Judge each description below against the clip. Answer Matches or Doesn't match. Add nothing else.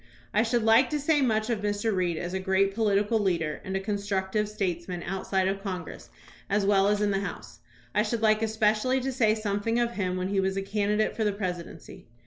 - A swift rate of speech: Matches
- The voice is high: Matches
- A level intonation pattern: Matches